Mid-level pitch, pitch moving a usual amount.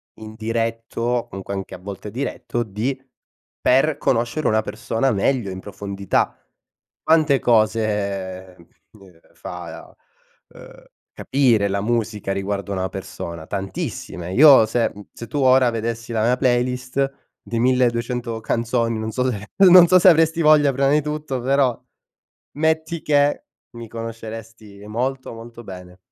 No: low, 115 Hz; average, 4.3 semitones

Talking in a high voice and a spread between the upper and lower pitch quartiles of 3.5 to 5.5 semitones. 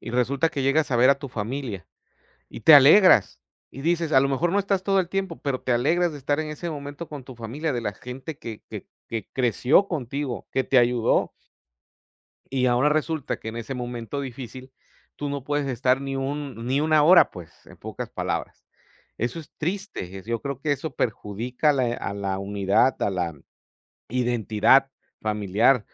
No: low, 135 Hz; average, 4.0 semitones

